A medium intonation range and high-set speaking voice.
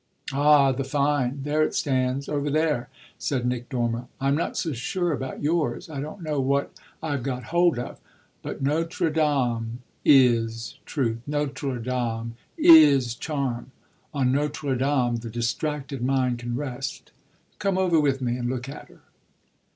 No: average, 3.3 semitones; low, 135 Hz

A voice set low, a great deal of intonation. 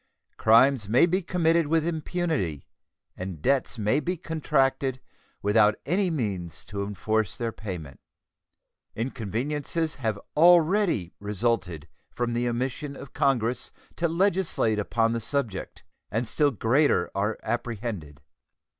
Yes: low, 120 Hz; wide, 6.5 semitones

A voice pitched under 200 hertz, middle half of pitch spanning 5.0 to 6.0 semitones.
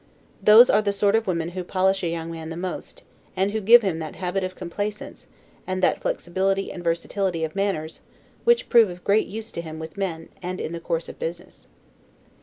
No: medium, 185 Hz; average, 3.2 semitones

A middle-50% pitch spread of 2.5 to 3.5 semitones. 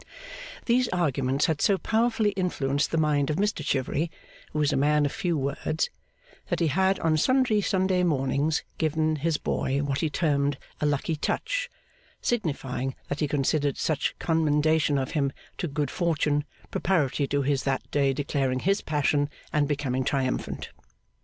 Yes: average, 3.2 semitones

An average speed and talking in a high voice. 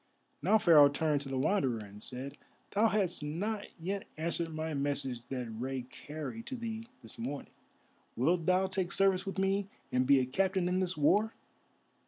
No: average, 175 wpm; medium, 160 Hz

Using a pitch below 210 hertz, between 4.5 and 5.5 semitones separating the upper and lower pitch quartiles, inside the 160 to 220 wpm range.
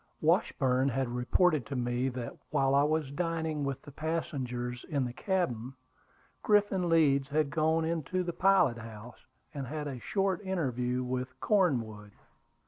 No: medium, 140 Hz; average, 4.8 semitones; average, 145 wpm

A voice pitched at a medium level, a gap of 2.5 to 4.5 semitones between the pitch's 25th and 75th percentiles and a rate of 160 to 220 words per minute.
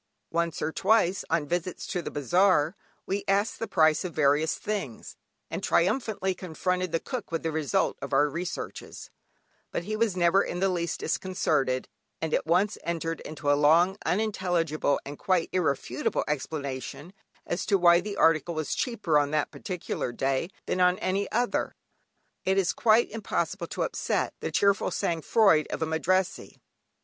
Yes: medium, 175 Hz; average, 3.5 semitones; average, 165 wpm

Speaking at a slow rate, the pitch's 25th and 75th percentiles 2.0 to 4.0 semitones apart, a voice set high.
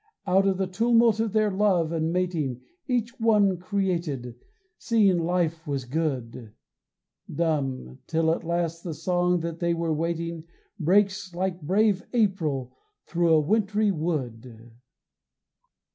No: slow, 130 wpm; average, 3.7 semitones; medium, 170 Hz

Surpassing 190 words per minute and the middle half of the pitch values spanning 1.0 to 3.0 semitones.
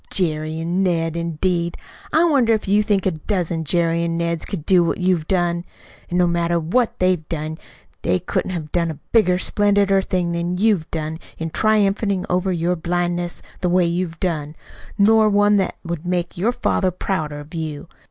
No: average, 180 wpm; average, 2.7 semitones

